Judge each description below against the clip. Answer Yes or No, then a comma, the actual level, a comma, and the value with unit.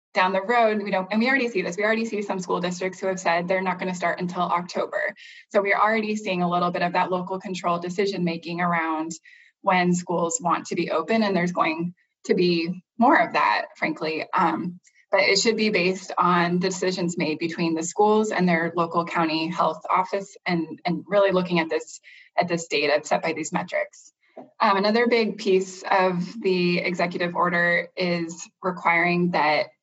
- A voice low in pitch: No, medium, 180 Hz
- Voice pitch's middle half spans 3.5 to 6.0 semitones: No, narrow, 2.4 semitones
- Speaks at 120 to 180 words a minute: No, average, 195 wpm